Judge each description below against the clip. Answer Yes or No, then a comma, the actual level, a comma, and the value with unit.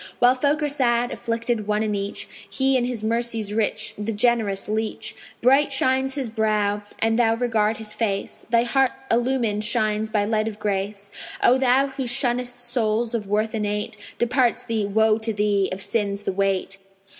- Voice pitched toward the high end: Yes, high, 225 Hz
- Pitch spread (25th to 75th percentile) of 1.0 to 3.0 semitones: Yes, average, 2.7 semitones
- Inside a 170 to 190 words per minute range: Yes, average, 175 wpm